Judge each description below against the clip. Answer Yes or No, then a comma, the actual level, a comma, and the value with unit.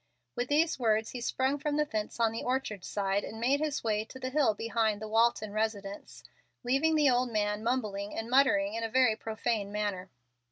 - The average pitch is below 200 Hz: No, high, 225 Hz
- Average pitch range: Yes, average, 3.6 semitones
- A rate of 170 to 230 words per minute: Yes, average, 200 wpm